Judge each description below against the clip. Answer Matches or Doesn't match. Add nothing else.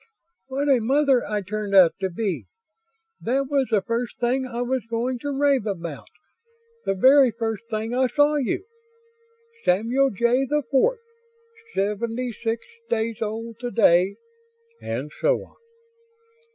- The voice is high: Matches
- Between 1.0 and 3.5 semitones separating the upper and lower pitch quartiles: Doesn't match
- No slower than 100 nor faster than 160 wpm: Matches